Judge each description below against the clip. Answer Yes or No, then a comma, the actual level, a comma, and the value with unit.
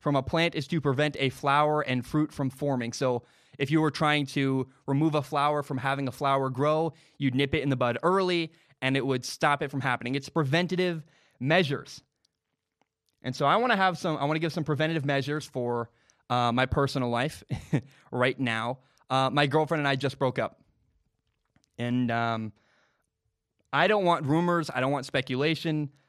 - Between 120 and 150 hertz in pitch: Yes, medium, 140 Hz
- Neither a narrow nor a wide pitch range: Yes, average, 3.1 semitones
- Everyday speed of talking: Yes, average, 190 wpm